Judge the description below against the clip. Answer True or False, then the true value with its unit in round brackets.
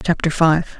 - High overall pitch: False (160 Hz)